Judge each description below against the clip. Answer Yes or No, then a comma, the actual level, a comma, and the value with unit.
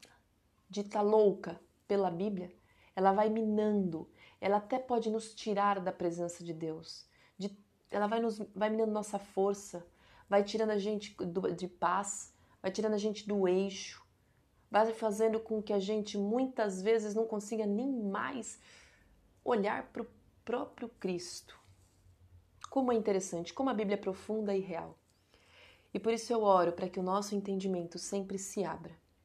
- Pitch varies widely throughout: No, average, 3.3 semitones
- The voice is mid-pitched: No, high, 200 Hz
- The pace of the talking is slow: No, average, 160 wpm